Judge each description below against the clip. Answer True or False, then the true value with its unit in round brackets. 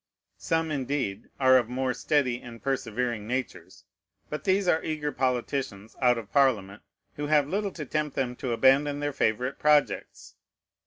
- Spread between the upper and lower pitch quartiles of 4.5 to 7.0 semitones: False (3.3 semitones)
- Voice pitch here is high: False (130 Hz)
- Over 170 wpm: False (155 wpm)